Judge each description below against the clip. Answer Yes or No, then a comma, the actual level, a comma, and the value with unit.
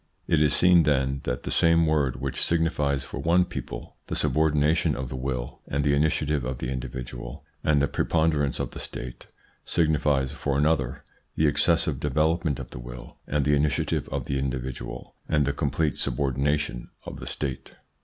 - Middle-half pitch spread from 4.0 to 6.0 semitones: No, average, 2.8 semitones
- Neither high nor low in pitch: No, very low, 70 Hz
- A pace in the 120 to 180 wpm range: Yes, average, 175 wpm